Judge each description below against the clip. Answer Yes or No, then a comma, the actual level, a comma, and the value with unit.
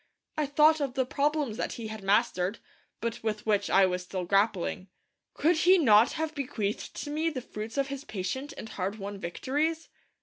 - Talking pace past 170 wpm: Yes, average, 190 wpm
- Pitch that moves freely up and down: Yes, wide, 6.4 semitones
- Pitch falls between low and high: No, high, 230 Hz